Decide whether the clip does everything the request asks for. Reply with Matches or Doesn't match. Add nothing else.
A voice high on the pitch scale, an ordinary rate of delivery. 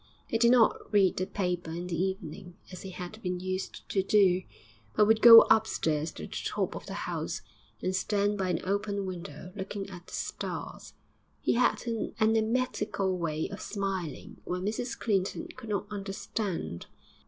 Matches